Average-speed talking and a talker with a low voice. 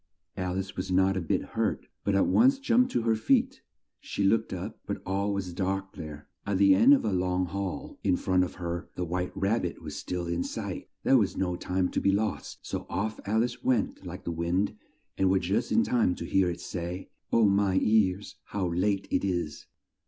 No: fast, 215 wpm; very low, 95 Hz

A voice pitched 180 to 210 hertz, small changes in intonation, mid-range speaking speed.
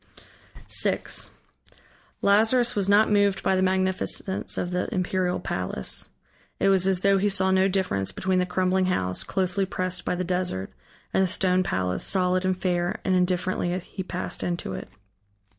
Yes: medium, 185 Hz; narrow, 1.2 semitones; average, 160 wpm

